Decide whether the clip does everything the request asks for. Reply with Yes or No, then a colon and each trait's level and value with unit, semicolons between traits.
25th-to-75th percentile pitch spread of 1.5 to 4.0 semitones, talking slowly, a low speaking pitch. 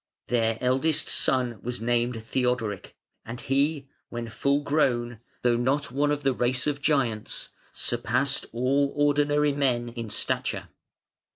Yes: average, 3.1 semitones; slow, 130 wpm; low, 125 Hz